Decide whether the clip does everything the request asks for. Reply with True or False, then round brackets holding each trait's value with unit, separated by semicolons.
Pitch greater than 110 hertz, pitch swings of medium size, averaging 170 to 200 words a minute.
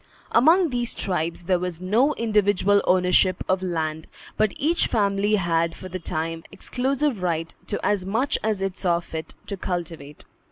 False (185 Hz; 4.0 semitones; 160 wpm)